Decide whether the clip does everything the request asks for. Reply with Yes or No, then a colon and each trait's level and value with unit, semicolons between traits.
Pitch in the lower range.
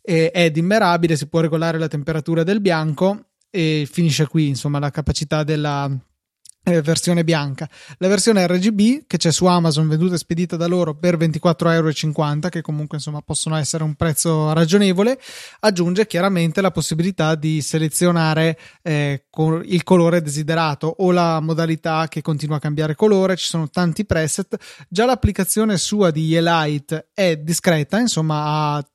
No: medium, 165 Hz